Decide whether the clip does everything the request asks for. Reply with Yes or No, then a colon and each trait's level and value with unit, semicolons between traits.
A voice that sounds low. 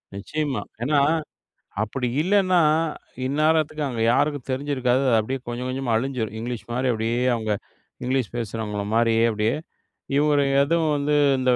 Yes: low, 130 Hz